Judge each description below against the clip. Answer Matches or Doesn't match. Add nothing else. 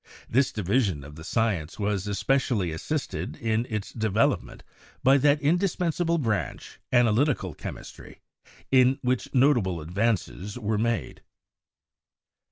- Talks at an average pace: Doesn't match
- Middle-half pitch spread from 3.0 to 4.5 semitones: Doesn't match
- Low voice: Matches